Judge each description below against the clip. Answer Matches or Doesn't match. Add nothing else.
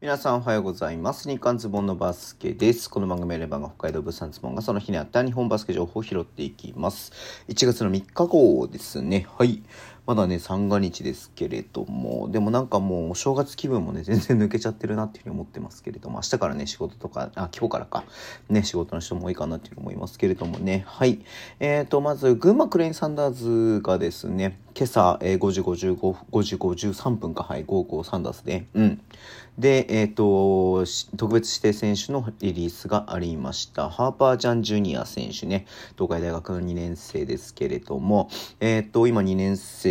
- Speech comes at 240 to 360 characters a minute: Doesn't match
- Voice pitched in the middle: Doesn't match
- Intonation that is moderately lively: Matches